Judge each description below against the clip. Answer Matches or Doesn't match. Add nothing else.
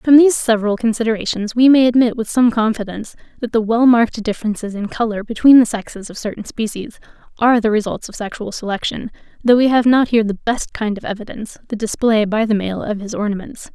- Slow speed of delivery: Doesn't match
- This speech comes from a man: Doesn't match